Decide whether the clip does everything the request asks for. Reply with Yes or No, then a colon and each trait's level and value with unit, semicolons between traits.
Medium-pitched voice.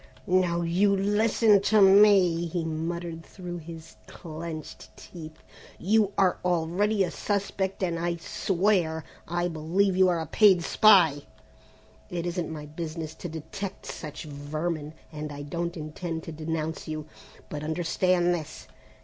Yes: medium, 170 Hz